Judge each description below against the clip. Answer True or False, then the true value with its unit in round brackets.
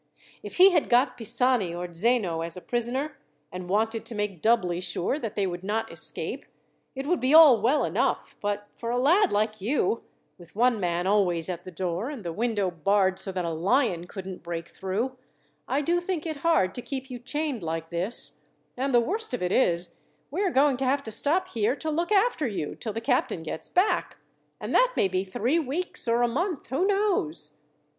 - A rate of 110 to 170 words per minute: False (205 wpm)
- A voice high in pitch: True (230 Hz)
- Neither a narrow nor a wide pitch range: False (7.2 semitones)